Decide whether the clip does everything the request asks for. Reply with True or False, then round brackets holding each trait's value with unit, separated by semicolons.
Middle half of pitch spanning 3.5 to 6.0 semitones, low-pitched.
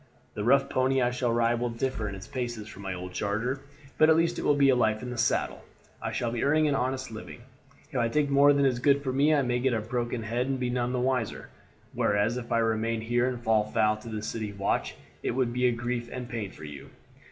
False (2.8 semitones; 120 Hz)